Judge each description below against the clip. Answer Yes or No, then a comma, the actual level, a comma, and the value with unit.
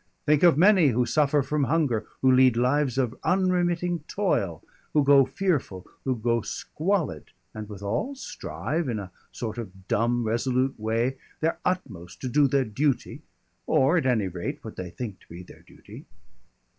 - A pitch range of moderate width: No, wide, 5.8 semitones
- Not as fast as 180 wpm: Yes, average, 165 wpm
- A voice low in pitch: Yes, low, 130 Hz